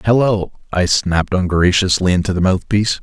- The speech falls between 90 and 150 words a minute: Yes, average, 140 wpm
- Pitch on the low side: Yes, very low, 95 Hz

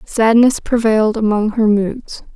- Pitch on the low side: No, high, 220 Hz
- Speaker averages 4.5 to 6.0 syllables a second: No, 4.2 syllables/s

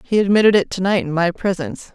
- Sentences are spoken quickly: Yes, fast, 215 wpm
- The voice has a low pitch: No, high, 190 Hz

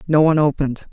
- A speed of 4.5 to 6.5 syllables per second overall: No, 8.5 syllables/s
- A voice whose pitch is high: No, medium, 145 Hz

